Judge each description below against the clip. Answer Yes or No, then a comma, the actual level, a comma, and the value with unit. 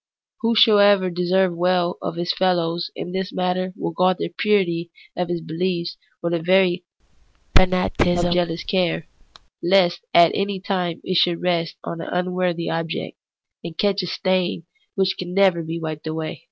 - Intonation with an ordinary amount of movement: No, narrow, 1.6 semitones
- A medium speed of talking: Yes, average, 165 wpm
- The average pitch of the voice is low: No, medium, 180 Hz